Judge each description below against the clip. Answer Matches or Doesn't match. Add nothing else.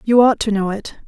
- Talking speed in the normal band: Doesn't match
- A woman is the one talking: Matches